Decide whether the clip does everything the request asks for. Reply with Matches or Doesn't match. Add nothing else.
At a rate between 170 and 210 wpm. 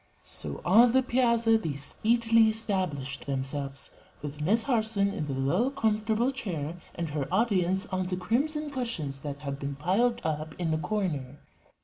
Doesn't match